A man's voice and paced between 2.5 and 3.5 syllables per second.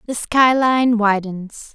No: female; 3.1 syllables/s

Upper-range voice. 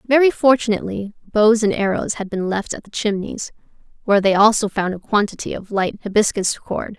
Yes: high, 210 Hz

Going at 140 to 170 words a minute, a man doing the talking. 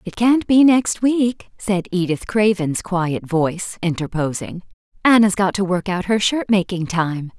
No: average, 160 wpm; female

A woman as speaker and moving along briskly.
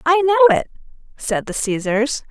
No: female; average, 155 wpm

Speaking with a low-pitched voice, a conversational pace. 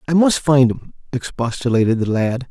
Yes: low, 130 Hz; average, 165 wpm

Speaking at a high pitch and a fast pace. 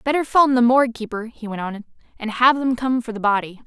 Yes: high, 240 Hz; fast, 245 wpm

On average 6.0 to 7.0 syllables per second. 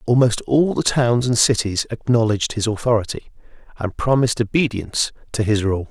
No: 5.5 syllables/s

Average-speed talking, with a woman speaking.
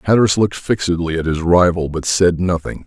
No: average, 190 wpm; male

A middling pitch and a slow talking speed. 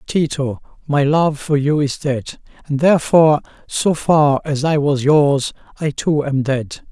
No: medium, 145 Hz; average, 165 wpm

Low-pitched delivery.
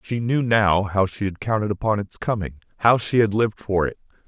Yes: low, 105 Hz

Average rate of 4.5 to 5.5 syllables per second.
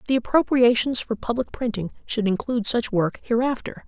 Yes: 5.4 syllables/s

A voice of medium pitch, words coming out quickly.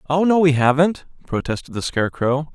No: medium, 145 Hz; average, 165 wpm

